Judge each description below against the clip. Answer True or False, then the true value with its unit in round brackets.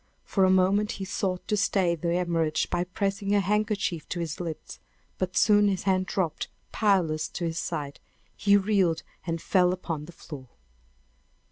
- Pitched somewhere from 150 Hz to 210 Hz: True (185 Hz)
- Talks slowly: False (165 wpm)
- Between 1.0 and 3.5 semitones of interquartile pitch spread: True (3.0 semitones)